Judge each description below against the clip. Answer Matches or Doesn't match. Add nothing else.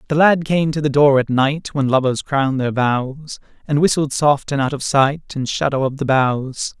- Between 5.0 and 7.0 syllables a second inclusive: Doesn't match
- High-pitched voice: Doesn't match